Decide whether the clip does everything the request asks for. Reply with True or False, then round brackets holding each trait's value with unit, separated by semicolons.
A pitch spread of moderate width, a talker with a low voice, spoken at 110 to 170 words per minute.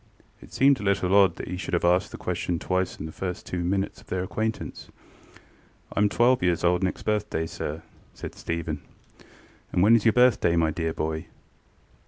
False (3.5 semitones; 90 Hz; 195 wpm)